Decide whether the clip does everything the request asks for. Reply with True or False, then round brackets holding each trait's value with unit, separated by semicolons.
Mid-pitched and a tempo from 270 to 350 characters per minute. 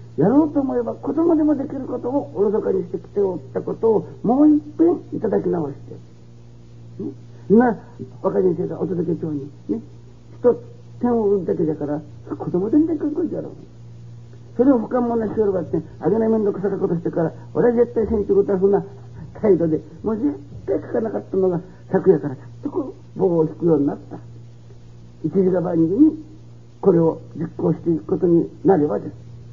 False (180 Hz; 365 characters per minute)